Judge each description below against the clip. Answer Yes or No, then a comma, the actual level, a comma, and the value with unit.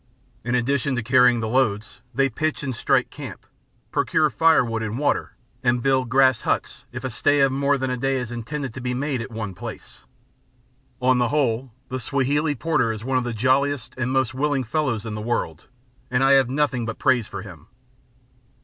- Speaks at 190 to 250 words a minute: Yes, average, 195 wpm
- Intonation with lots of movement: No, average, 2.9 semitones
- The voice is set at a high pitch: No, low, 130 Hz